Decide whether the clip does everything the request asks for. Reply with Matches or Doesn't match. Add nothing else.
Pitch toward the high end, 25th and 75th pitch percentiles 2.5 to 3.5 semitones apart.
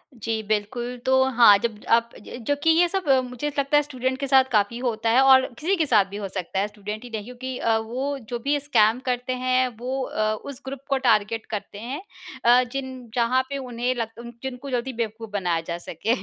Matches